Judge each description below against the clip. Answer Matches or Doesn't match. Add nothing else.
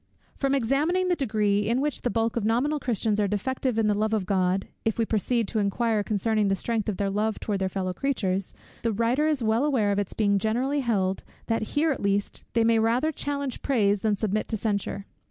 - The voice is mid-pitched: Doesn't match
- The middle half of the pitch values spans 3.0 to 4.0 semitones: Matches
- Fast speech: Matches